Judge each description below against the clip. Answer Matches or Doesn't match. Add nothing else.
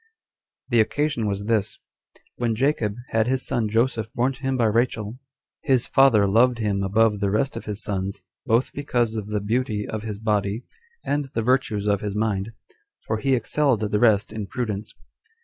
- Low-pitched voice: Matches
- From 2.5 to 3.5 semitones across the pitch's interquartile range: Matches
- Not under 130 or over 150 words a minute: Doesn't match